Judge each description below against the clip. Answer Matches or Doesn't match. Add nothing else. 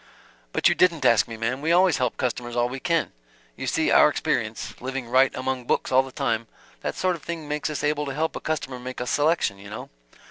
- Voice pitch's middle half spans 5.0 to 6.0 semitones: Doesn't match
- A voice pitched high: Doesn't match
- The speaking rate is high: Matches